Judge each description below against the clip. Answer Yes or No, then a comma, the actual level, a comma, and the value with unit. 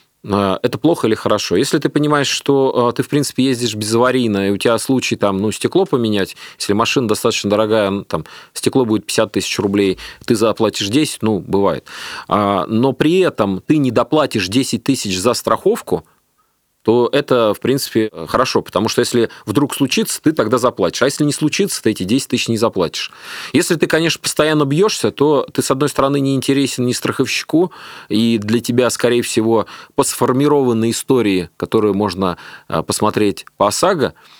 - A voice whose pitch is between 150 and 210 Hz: No, low, 120 Hz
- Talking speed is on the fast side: Yes, fast, 170 wpm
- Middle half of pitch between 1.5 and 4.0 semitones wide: No, average, 4.6 semitones